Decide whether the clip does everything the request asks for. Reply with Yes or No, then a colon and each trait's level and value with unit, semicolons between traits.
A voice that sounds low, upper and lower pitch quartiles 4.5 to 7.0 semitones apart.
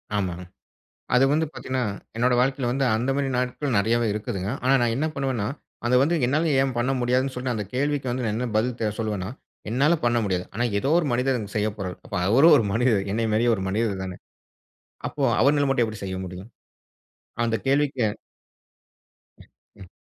No: low, 120 Hz; average, 4.0 semitones